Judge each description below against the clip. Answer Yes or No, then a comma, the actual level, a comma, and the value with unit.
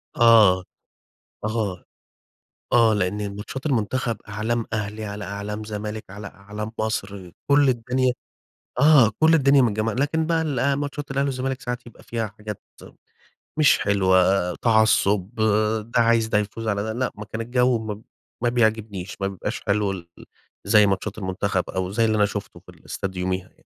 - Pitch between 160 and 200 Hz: No, low, 110 Hz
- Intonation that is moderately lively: Yes, average, 3.3 semitones